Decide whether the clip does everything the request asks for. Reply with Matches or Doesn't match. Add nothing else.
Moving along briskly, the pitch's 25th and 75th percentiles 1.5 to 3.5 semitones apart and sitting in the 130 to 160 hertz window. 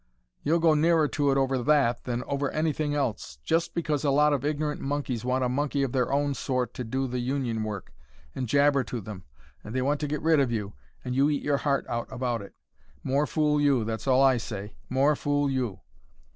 Matches